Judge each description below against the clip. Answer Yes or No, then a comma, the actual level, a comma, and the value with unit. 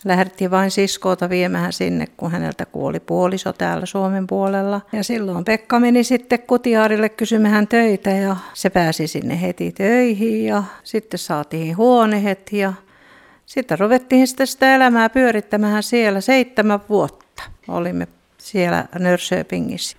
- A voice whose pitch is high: Yes, high, 200 Hz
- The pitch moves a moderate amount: Yes, average, 3.9 semitones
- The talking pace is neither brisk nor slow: Yes, average, 130 wpm